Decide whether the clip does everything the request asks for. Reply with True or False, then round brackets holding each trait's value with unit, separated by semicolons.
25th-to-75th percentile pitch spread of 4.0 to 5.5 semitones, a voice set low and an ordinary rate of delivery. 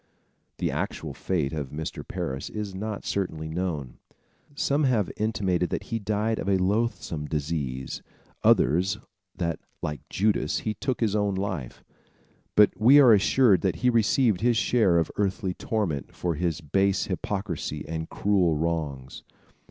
True (5.1 semitones; 95 Hz; 145 wpm)